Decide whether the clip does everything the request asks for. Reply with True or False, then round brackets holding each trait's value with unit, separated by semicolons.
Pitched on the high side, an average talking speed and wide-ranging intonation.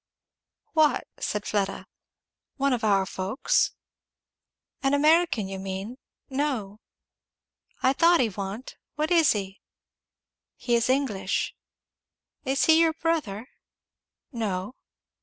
False (245 Hz; 105 wpm; 6.9 semitones)